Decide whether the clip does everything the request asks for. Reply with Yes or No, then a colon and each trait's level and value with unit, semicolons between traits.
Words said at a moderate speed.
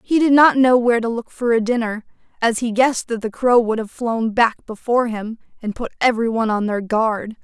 No: fast, 235 wpm